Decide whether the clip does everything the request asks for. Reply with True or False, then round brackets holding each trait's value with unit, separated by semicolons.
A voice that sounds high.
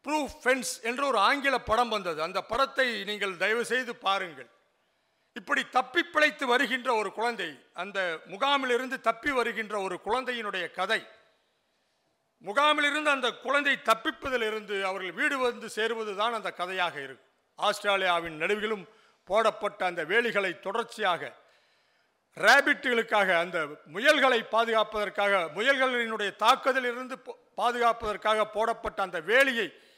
True (230 Hz)